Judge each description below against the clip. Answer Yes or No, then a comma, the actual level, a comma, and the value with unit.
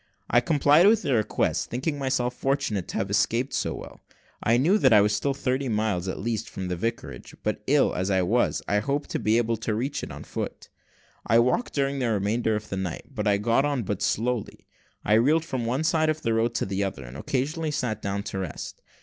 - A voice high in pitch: No, low, 115 Hz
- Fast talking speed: Yes, fast, 225 wpm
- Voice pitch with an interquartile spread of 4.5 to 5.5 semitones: Yes, average, 4.9 semitones